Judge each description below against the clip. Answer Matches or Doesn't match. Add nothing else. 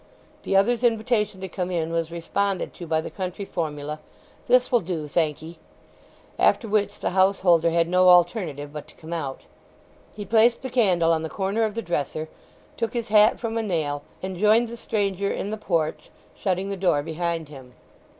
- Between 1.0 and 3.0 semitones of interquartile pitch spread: Doesn't match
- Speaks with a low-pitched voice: Doesn't match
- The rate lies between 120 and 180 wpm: Doesn't match